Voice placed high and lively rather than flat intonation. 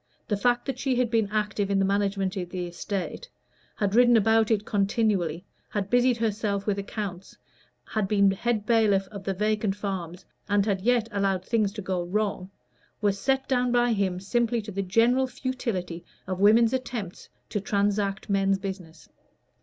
No: high, 205 Hz; average, 2.8 semitones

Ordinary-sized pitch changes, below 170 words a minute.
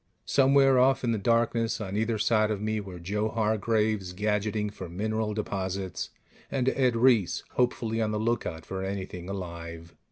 Yes: average, 3.2 semitones; average, 160 wpm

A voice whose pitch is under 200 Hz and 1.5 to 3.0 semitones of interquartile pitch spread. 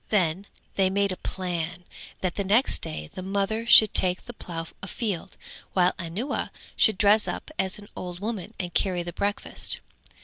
Yes: high, 190 Hz; narrow, 2.6 semitones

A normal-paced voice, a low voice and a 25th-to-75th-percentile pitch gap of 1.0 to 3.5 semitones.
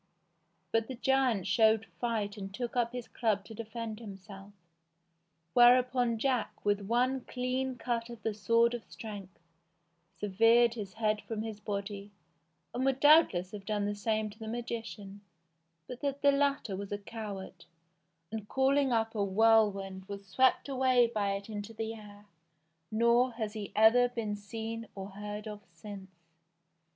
No: average, 155 wpm; high, 220 Hz; average, 2.9 semitones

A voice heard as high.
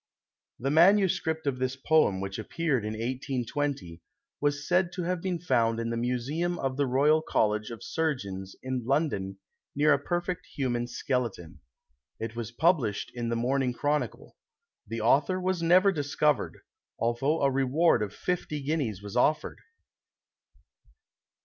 No: low, 135 Hz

